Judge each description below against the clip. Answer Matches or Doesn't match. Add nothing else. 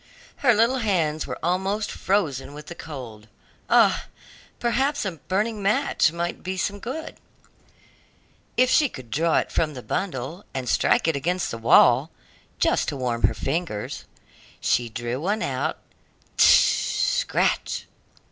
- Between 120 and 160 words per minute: Matches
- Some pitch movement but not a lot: Doesn't match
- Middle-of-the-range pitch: Matches